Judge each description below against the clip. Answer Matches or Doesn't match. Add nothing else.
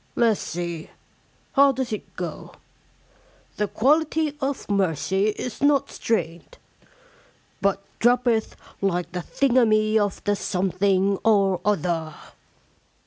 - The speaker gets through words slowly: Matches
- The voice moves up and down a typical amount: Matches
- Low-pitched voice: Doesn't match